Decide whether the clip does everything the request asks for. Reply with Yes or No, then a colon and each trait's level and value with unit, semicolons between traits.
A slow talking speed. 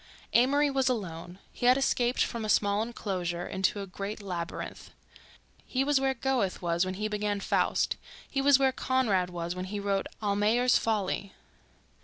No: average, 160 wpm